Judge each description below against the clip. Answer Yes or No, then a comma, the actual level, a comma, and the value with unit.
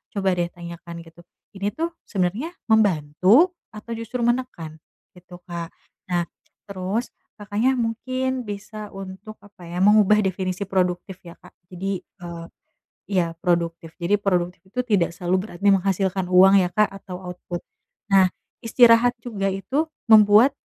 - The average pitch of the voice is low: No, high, 195 Hz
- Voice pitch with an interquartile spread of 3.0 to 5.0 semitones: Yes, average, 3.4 semitones